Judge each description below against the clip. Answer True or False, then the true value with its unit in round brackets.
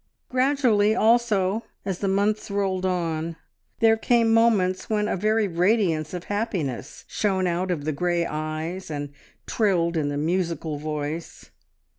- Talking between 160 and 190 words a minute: False (140 wpm)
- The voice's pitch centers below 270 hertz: True (185 Hz)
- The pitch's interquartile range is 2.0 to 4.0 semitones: False (4.7 semitones)